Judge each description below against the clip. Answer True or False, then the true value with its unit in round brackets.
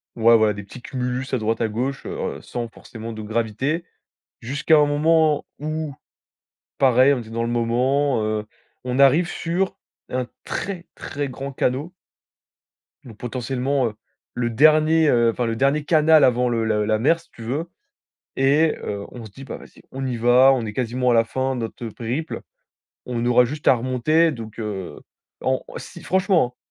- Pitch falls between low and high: False (125 Hz)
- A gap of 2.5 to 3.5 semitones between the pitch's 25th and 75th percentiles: False (4.0 semitones)